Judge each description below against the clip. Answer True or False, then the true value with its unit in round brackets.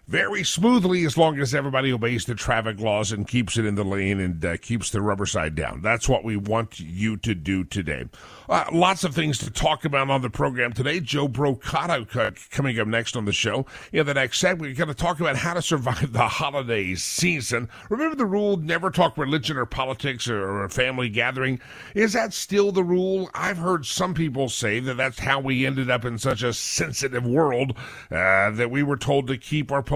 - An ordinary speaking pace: False (210 wpm)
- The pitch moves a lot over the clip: True (6.0 semitones)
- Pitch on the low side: True (130 Hz)